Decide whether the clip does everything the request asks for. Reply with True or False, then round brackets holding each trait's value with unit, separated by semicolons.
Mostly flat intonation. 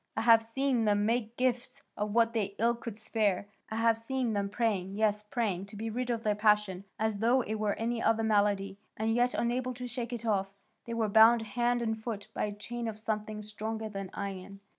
True (2.3 semitones)